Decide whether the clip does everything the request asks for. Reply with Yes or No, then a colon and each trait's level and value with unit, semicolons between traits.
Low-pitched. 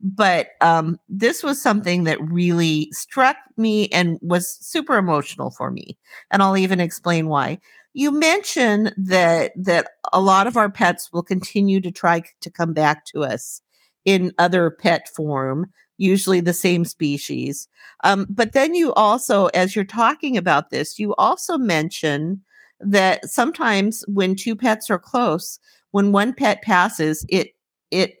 No: high, 190 Hz